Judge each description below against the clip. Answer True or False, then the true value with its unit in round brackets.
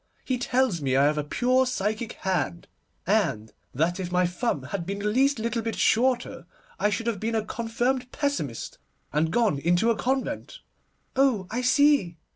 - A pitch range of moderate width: False (6.2 semitones)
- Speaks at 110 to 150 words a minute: False (175 wpm)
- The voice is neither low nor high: False (220 Hz)